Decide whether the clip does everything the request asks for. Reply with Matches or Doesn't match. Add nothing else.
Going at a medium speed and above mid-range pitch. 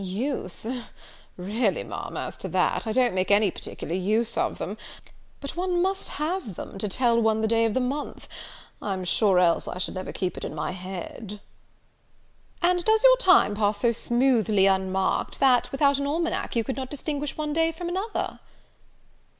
Matches